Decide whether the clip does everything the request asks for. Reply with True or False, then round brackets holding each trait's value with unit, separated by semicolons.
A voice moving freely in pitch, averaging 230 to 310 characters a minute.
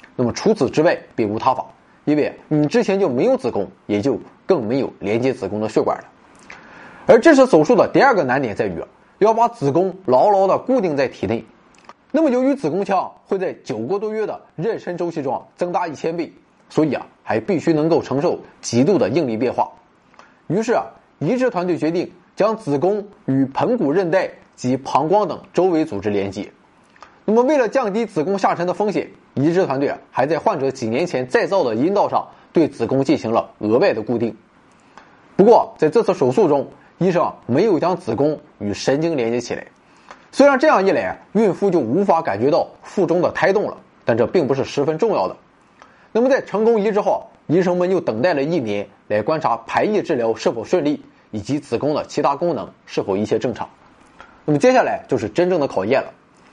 True (8.2 semitones; 290 characters per minute)